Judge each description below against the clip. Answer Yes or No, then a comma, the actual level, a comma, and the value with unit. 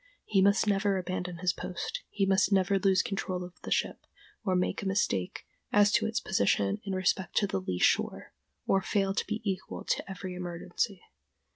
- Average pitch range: No, narrow, 1.9 semitones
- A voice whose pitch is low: No, high, 190 Hz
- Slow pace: No, average, 190 wpm